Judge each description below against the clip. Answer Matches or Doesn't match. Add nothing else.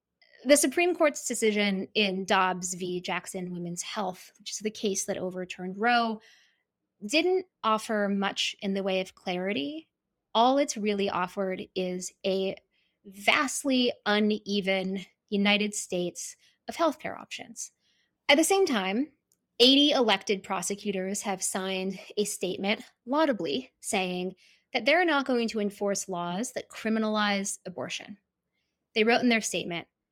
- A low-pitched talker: Doesn't match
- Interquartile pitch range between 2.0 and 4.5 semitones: Matches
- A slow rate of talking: Matches